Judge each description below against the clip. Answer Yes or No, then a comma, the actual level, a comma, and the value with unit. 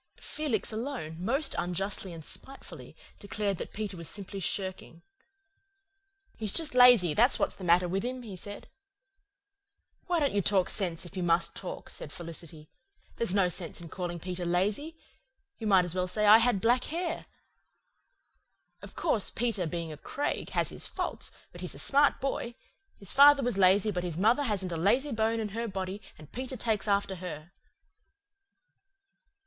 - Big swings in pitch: No, average, 4.8 semitones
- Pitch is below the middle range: No, high, 200 Hz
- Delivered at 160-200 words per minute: Yes, average, 170 wpm